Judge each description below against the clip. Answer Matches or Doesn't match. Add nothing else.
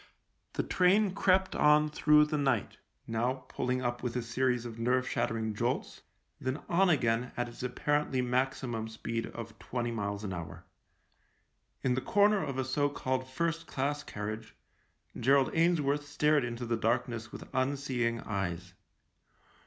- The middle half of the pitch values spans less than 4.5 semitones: Matches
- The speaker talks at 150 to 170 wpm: Matches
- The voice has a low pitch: Matches